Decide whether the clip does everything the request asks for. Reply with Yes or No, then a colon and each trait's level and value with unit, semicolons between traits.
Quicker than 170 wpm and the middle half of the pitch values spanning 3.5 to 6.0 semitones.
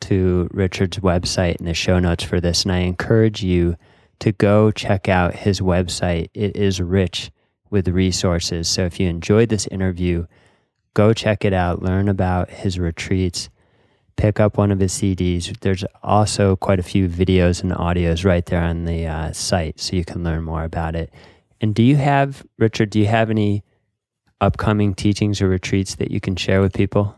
No: average, 185 wpm; average, 2.8 semitones